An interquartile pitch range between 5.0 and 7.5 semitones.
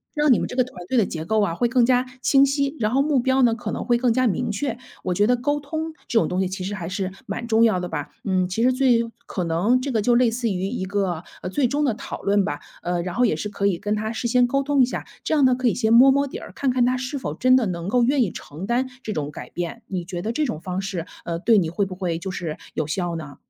Yes: wide, 5.6 semitones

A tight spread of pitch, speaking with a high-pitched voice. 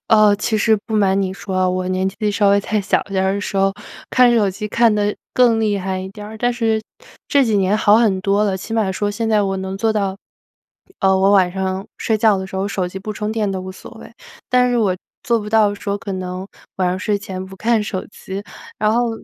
Yes: narrow, 2.3 semitones; high, 205 Hz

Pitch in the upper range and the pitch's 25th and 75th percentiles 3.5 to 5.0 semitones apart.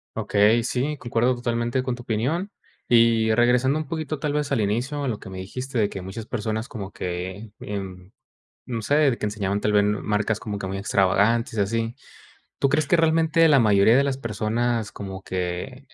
No: low, 115 Hz; average, 4.3 semitones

